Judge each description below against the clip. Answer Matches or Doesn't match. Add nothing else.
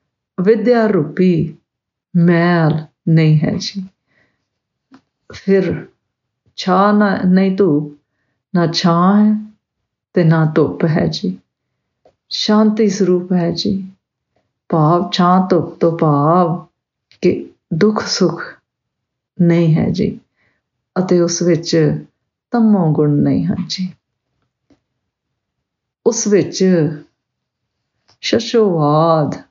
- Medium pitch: Matches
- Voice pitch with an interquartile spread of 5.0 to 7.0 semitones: Doesn't match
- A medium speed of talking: Doesn't match